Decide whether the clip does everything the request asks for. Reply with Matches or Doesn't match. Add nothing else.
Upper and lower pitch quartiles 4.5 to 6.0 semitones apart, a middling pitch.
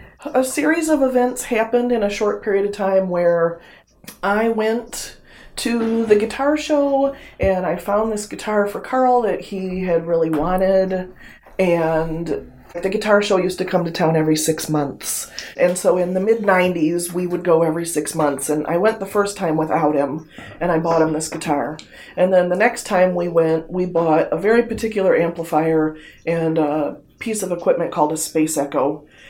Matches